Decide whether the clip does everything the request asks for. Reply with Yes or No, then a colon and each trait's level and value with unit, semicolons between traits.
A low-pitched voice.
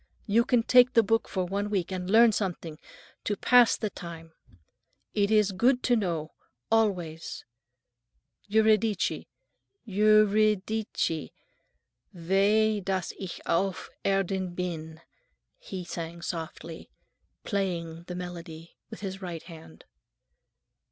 No: high, 190 Hz